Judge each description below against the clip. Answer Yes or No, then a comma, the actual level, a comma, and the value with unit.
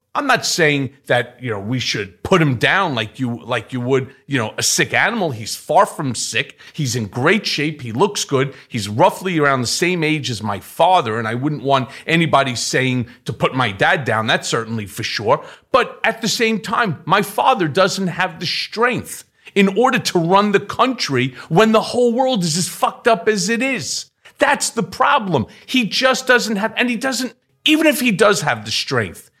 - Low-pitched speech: No, medium, 170 Hz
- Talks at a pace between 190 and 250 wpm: Yes, fast, 205 wpm